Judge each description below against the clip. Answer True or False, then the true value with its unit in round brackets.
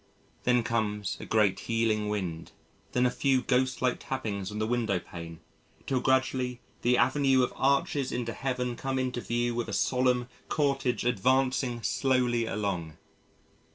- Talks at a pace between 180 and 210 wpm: False (150 wpm)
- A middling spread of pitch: True (3.1 semitones)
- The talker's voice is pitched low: True (125 Hz)